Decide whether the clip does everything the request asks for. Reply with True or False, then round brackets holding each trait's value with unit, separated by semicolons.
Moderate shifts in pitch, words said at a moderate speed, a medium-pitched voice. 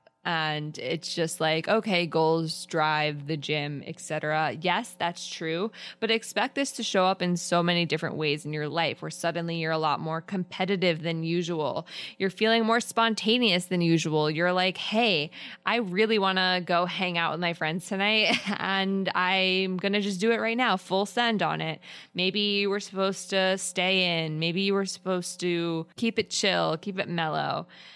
True (3.5 semitones; 185 wpm; 180 Hz)